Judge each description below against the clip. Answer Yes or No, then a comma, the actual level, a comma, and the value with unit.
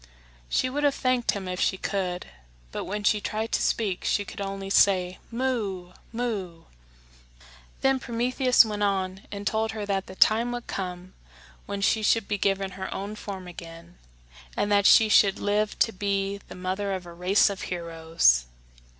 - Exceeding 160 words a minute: Yes, average, 175 wpm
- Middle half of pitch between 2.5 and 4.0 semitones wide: Yes, average, 2.8 semitones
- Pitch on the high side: Yes, high, 200 Hz